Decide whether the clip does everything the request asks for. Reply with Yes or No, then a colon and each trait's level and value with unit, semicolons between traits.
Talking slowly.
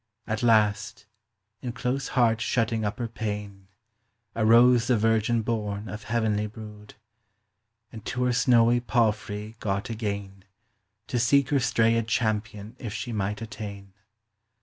Yes: slow, 130 wpm